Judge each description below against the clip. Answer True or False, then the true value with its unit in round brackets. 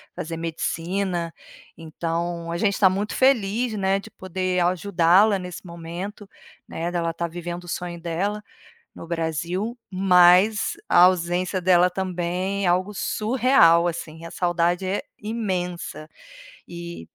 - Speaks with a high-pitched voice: False (180 Hz)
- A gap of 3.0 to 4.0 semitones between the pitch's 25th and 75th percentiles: False (2.4 semitones)